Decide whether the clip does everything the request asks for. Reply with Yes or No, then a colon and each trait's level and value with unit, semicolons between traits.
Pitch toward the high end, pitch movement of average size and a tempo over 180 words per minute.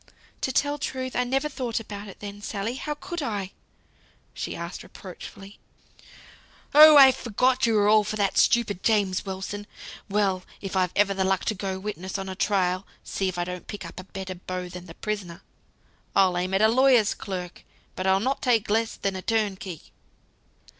Yes: high, 205 Hz; average, 3.5 semitones; average, 190 wpm